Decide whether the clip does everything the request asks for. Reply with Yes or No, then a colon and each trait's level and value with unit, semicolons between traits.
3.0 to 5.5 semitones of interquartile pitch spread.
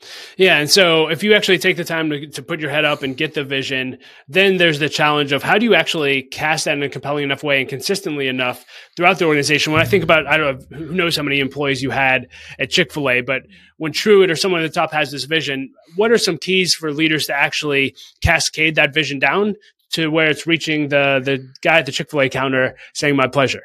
Yes: average, 3.5 semitones